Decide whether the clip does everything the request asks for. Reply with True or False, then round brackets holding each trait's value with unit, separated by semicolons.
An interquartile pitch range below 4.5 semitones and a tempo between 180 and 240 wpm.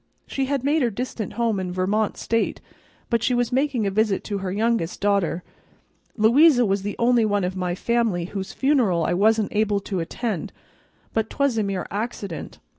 True (3.7 semitones; 185 wpm)